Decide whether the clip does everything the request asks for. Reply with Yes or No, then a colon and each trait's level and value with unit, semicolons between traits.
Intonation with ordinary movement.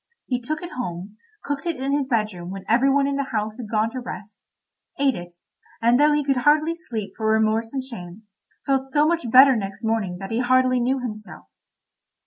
Yes: average, 4.2 semitones